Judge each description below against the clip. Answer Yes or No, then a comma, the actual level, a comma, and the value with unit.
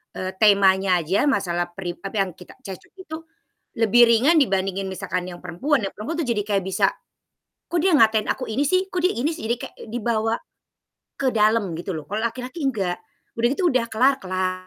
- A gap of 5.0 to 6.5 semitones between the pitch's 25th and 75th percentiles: Yes, wide, 5.6 semitones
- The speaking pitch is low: No, high, 220 Hz